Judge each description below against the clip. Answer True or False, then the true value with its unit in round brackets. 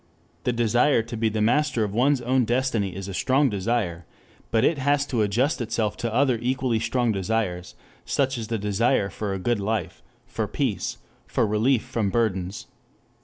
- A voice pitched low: True (115 Hz)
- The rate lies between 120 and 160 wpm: False (175 wpm)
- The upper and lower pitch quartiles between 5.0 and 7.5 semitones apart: False (3.5 semitones)